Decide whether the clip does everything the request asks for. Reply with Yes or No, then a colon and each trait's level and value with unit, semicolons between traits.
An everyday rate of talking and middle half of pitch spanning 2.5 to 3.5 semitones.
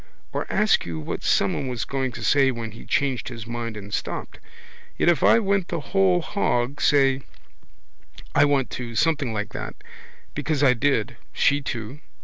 No: average, 170 wpm; average, 4.0 semitones